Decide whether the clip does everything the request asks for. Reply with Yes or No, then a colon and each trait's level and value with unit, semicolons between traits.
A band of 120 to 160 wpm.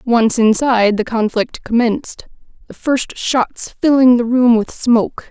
Yes: average, 145 wpm